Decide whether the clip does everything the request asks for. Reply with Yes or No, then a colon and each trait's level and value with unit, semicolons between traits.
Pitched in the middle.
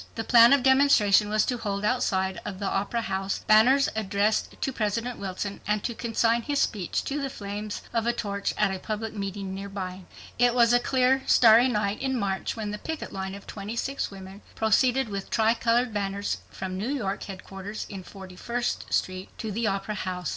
No: high, 210 Hz